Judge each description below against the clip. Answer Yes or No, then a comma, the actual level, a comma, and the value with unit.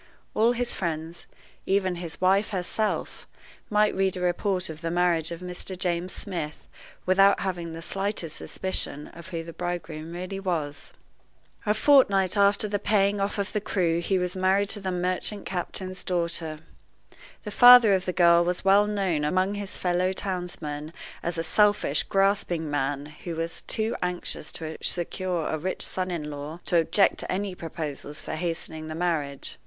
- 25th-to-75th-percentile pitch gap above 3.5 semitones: No, average, 2.9 semitones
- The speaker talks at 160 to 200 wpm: Yes, average, 170 wpm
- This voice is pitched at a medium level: Yes, medium, 180 Hz